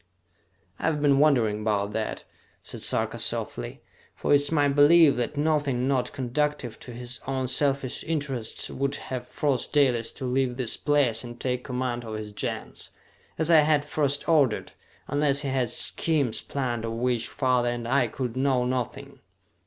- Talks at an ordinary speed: Yes, average, 170 wpm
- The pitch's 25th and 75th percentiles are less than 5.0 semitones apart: Yes, average, 3.1 semitones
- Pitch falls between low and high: No, low, 130 Hz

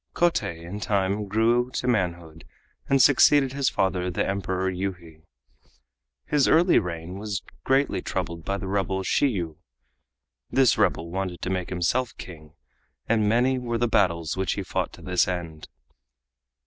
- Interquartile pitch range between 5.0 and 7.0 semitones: Yes, average, 5.3 semitones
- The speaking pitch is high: No, very low, 95 Hz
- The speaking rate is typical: Yes, average, 150 wpm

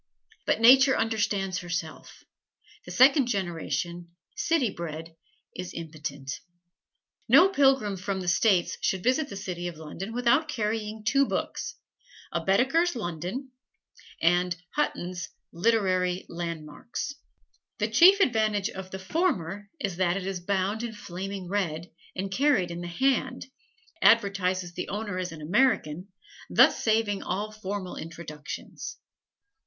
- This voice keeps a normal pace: No, slow, 125 wpm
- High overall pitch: Yes, high, 195 Hz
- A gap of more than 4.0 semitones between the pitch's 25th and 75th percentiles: Yes, average, 4.7 semitones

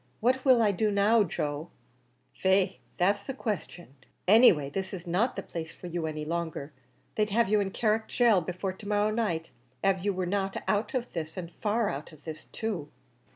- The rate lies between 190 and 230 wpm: Yes, average, 200 wpm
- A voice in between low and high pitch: No, high, 195 Hz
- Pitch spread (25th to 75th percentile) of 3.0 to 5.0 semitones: Yes, average, 4.0 semitones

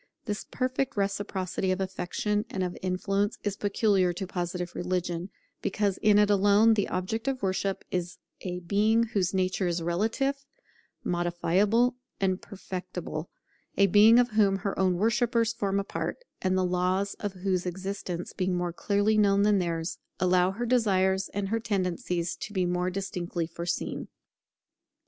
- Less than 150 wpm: No, average, 155 wpm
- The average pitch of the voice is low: No, high, 190 Hz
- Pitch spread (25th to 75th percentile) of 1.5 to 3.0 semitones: Yes, narrow, 2.4 semitones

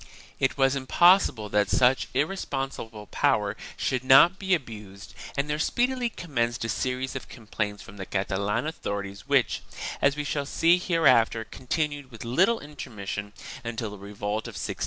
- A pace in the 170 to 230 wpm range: No, average, 155 wpm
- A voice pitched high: No, low, 125 Hz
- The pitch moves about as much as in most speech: No, wide, 6.1 semitones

